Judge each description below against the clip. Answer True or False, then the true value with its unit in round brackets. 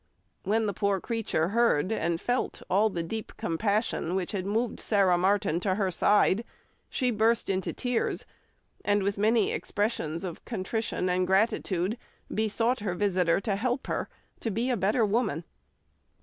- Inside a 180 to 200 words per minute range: False (155 wpm)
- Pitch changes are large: False (3.3 semitones)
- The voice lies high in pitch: True (205 Hz)